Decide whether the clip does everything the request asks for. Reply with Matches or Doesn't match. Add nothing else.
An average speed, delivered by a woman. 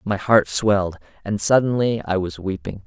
Doesn't match